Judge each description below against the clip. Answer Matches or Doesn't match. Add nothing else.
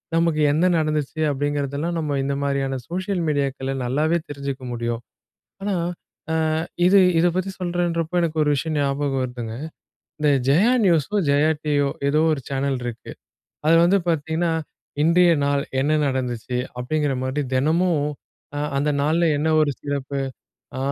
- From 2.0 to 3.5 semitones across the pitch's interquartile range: Matches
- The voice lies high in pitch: Doesn't match